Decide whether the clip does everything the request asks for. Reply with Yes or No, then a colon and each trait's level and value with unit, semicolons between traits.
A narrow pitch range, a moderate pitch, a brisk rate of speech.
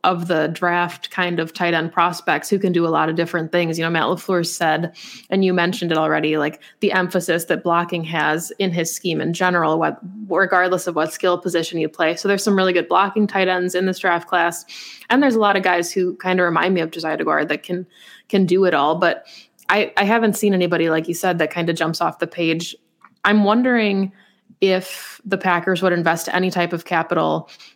Yes: narrow, 2.1 semitones; medium, 175 Hz; fast, 225 wpm